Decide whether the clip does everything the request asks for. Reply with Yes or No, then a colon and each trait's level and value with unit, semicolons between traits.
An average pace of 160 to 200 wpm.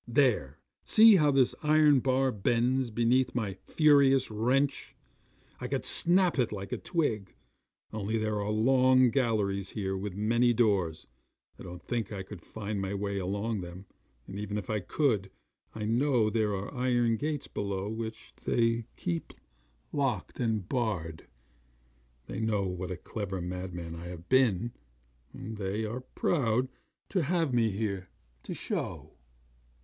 No: average, 150 wpm